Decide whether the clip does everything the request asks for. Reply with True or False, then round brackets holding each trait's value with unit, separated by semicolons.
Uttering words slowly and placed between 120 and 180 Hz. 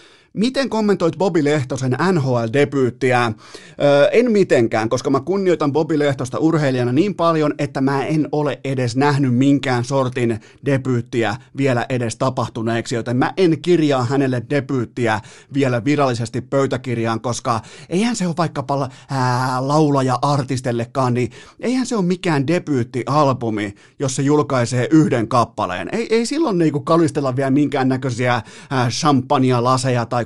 False (125 wpm; 135 Hz)